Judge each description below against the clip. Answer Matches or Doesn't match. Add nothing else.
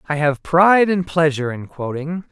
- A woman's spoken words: Doesn't match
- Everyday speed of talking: Matches